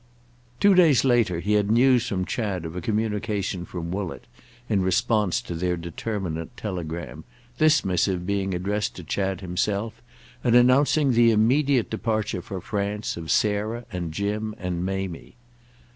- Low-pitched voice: Yes, low, 100 Hz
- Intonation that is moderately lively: Yes, average, 3.8 semitones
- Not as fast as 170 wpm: Yes, average, 145 wpm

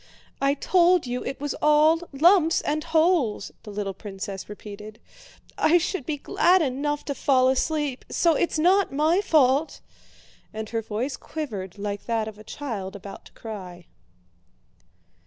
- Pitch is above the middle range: Yes, very high, 275 Hz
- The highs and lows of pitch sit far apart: Yes, wide, 6.8 semitones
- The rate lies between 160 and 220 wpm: No, average, 150 wpm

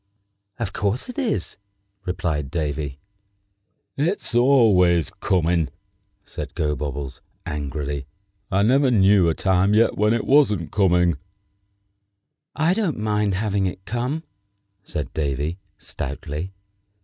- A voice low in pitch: Yes, very low, 95 Hz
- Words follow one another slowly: Yes, slow, 110 wpm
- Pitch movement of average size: No, wide, 6.5 semitones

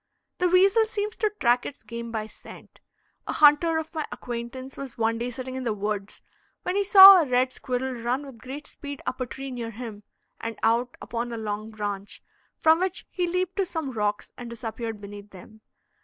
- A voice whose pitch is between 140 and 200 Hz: No, very high, 250 Hz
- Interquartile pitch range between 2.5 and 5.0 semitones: No, wide, 5.6 semitones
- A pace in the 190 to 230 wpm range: Yes, average, 200 wpm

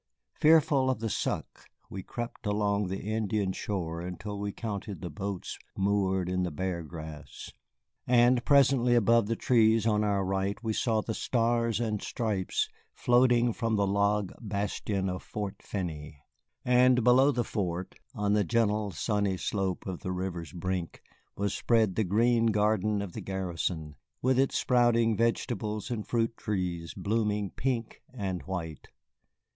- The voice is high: No, low, 105 Hz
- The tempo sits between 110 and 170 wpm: Yes, average, 150 wpm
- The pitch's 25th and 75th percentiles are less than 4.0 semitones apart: Yes, average, 3.6 semitones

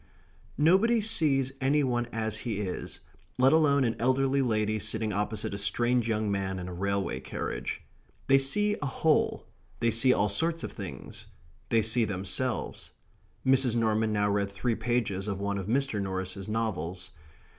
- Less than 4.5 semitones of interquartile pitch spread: No, average, 4.8 semitones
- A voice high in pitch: No, low, 110 Hz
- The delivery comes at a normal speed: Yes, average, 160 wpm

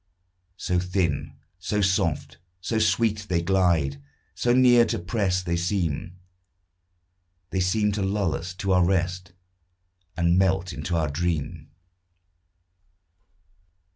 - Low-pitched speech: Yes, very low, 90 Hz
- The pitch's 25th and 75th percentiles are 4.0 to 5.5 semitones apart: No, narrow, 2.4 semitones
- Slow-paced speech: Yes, slow, 115 wpm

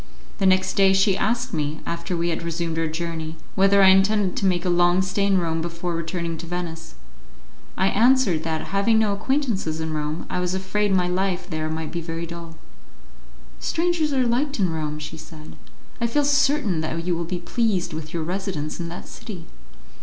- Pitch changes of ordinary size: Yes, average, 3.4 semitones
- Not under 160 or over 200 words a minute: Yes, average, 195 wpm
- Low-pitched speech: No, medium, 180 Hz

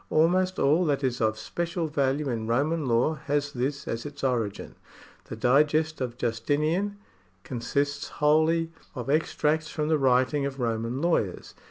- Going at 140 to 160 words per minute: Yes, average, 155 wpm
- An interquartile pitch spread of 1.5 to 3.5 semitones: No, average, 4.1 semitones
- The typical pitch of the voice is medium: Yes, medium, 145 Hz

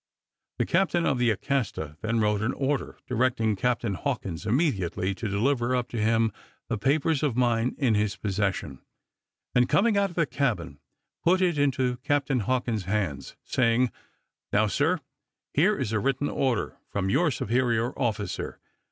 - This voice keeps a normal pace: Yes, average, 155 wpm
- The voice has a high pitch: No, low, 120 Hz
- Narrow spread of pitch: No, average, 4.7 semitones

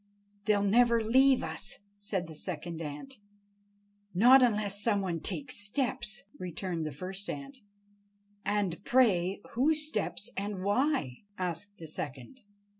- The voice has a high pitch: Yes, high, 205 Hz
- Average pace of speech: No, slow, 125 wpm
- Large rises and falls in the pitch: Yes, wide, 5.7 semitones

